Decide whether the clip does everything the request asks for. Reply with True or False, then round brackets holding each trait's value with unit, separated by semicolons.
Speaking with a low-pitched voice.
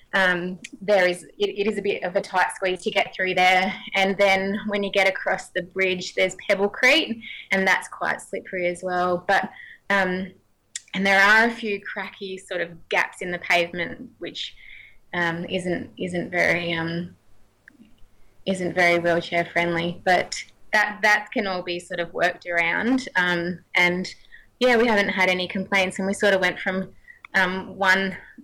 False (190 Hz)